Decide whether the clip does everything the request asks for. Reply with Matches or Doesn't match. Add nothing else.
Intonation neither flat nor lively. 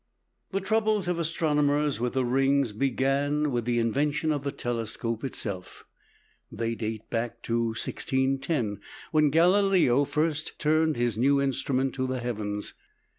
Matches